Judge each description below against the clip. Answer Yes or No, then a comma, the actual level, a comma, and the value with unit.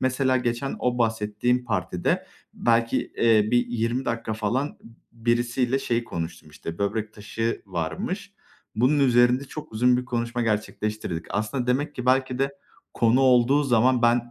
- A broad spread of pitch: No, narrow, 2.4 semitones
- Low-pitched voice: Yes, low, 120 Hz